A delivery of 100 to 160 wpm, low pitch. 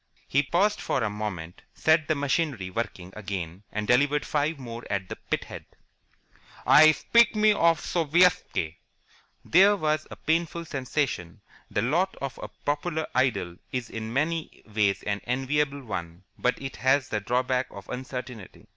Yes: average, 150 wpm; low, 130 Hz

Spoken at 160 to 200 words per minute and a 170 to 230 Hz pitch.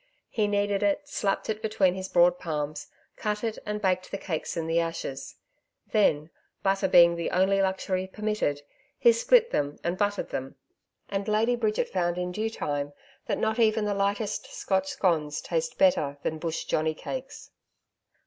Yes: average, 170 wpm; high, 190 Hz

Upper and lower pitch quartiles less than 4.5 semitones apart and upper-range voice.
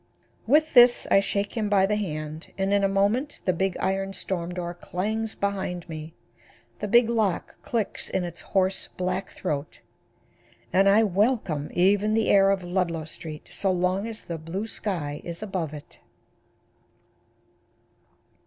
Yes: average, 3.1 semitones; high, 195 Hz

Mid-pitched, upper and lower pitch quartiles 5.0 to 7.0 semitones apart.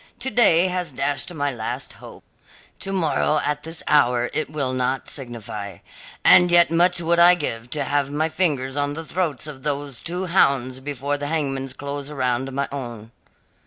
No: medium, 145 Hz; average, 3.8 semitones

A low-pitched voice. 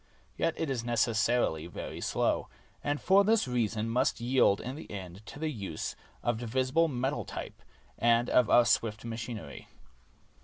Yes: low, 120 Hz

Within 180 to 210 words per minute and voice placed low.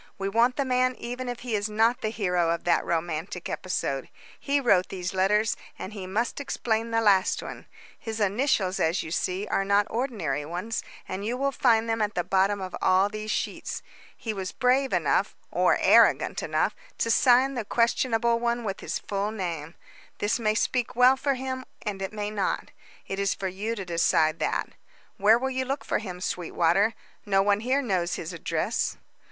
No: average, 190 wpm; high, 210 Hz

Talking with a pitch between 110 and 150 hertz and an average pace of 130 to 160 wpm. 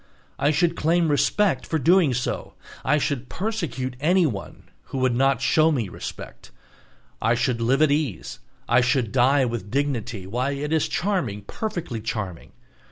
Yes: low, 135 Hz; average, 155 wpm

